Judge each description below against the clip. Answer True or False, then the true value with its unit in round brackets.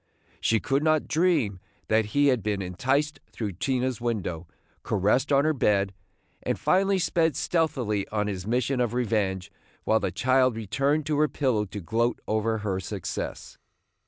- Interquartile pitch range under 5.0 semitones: False (5.4 semitones)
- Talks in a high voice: False (115 Hz)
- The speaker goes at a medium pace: True (160 wpm)